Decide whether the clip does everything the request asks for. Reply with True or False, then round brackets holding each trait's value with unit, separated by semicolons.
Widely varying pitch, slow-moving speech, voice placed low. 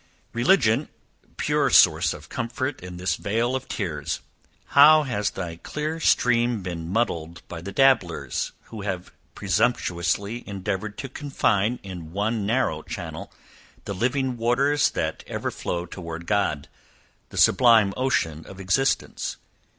True (5.7 semitones; 130 wpm; 105 Hz)